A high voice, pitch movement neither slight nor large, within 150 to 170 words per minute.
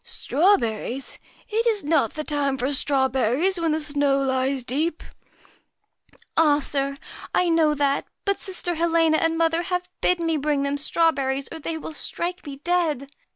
No: very high, 300 Hz; average, 3.3 semitones; average, 185 wpm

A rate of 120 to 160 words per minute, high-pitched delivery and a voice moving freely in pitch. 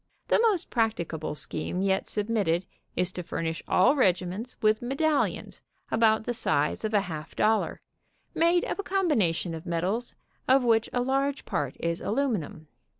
Yes: average, 155 wpm; high, 215 Hz; wide, 6.6 semitones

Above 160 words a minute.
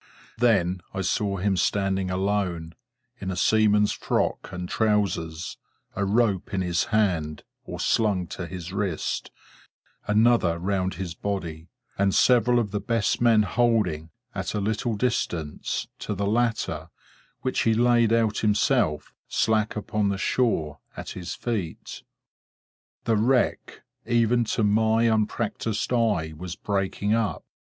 No: slow, 135 wpm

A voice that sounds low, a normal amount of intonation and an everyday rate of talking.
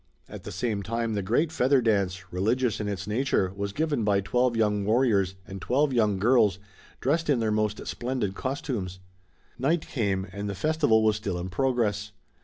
Yes: low, 110 Hz; average, 4.2 semitones; average, 180 wpm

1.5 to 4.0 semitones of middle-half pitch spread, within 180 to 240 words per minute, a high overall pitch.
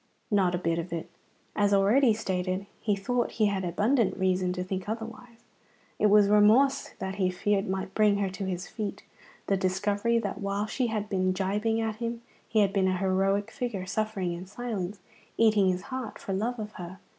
Yes: average, 2.7 semitones; average, 190 wpm; high, 200 Hz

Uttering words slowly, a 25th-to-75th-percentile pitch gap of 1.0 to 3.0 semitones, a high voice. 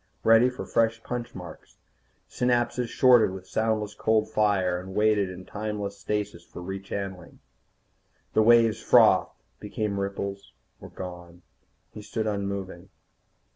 No: slow, 125 wpm; average, 2.7 semitones; low, 105 Hz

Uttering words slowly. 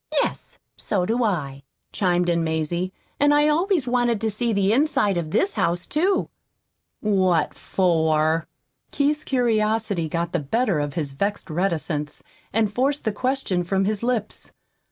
No: average, 150 wpm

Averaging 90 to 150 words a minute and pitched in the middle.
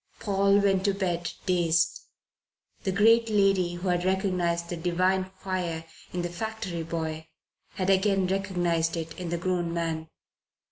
Yes: average, 145 wpm; medium, 180 Hz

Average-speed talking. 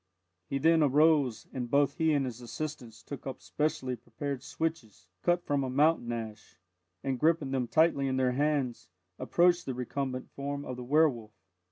Yes: average, 170 wpm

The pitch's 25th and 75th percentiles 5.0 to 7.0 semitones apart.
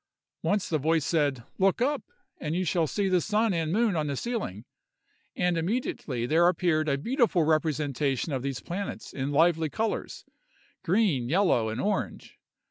Yes: average, 5.3 semitones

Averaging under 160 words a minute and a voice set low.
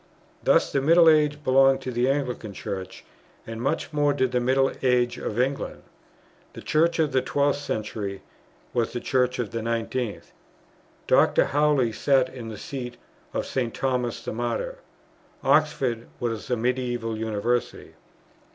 Yes: average, 150 wpm; low, 125 Hz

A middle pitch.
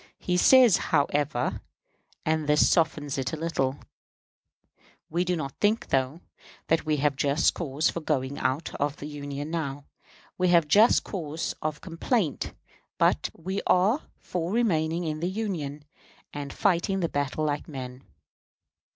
Yes: medium, 155 Hz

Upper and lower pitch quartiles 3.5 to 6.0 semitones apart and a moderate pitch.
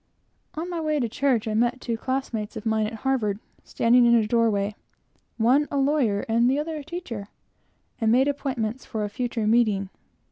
No: average, 3.8 semitones; high, 235 Hz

